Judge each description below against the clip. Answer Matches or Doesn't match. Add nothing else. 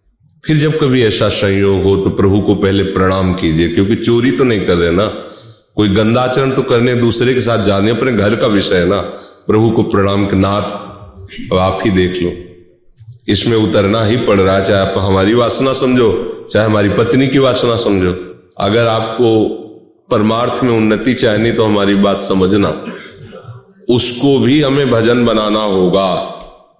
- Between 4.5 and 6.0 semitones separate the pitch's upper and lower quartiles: Doesn't match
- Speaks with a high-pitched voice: Doesn't match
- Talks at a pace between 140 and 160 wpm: Doesn't match